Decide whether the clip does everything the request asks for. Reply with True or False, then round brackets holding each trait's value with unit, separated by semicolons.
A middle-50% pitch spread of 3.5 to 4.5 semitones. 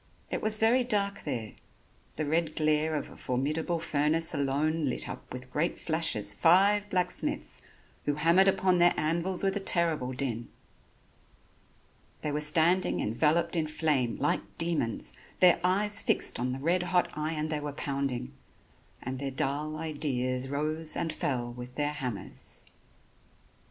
True (3.9 semitones)